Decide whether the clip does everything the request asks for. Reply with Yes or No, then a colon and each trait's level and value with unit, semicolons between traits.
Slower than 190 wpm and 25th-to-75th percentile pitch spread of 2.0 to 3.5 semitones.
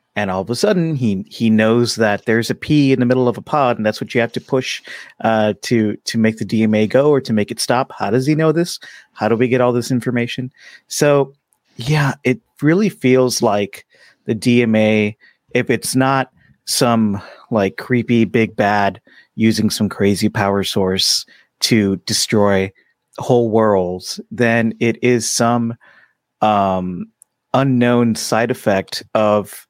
Yes: average, 170 wpm; average, 3.1 semitones